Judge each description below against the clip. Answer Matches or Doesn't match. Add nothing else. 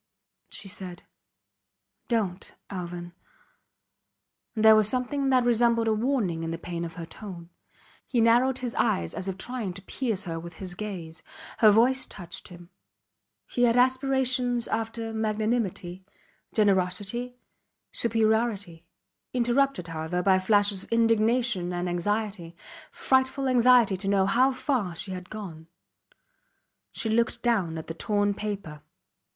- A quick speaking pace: Doesn't match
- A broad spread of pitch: Doesn't match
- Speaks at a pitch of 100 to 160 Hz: Doesn't match